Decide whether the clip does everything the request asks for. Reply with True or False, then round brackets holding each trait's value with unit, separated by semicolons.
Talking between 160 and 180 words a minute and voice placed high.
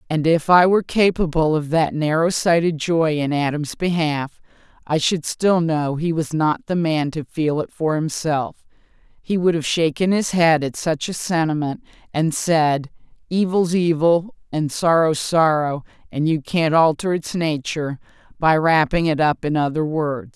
False (170 wpm; 160 Hz)